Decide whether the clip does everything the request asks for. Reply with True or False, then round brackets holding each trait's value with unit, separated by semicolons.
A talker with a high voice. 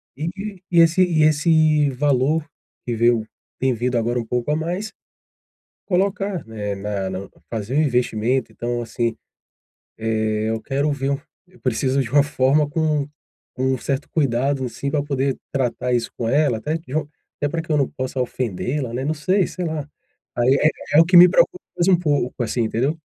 False (140 Hz)